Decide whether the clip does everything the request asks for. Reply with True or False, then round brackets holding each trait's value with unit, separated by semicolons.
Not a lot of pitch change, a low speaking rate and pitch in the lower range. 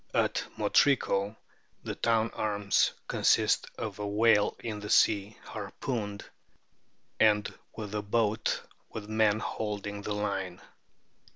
True (1.3 semitones; 115 wpm; 105 Hz)